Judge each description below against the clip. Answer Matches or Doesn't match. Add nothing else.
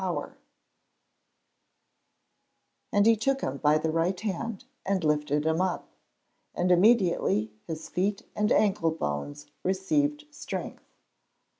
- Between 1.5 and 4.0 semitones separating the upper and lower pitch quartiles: Doesn't match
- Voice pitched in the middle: Matches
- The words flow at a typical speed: Doesn't match